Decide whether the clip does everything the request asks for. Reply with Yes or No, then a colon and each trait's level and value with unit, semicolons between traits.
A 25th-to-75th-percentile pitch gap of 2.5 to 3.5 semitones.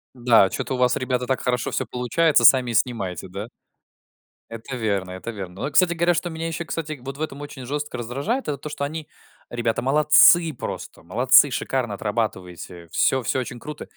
No: average, 4.7 semitones